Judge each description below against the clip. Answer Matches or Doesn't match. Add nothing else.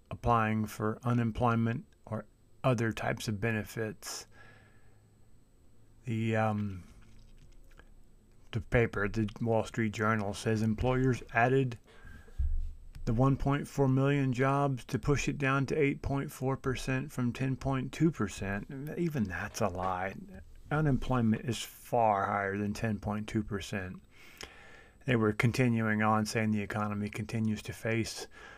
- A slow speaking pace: Matches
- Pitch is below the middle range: Matches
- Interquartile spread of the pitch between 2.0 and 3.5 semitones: Matches